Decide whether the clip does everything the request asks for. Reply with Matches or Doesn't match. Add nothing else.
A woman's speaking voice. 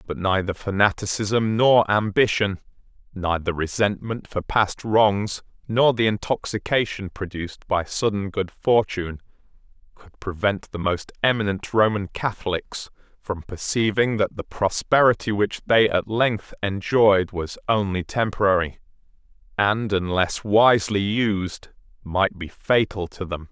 Doesn't match